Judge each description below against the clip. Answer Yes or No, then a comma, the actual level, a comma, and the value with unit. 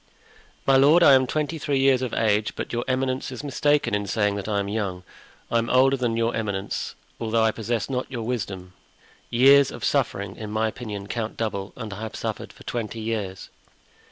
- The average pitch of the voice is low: Yes, low, 115 Hz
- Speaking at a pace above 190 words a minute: Yes, average, 200 wpm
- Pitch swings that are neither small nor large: Yes, average, 3.8 semitones